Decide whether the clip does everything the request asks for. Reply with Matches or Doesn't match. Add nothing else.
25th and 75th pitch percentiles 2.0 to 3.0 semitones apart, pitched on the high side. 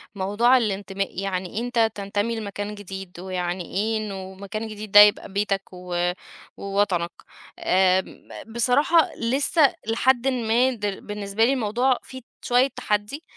Doesn't match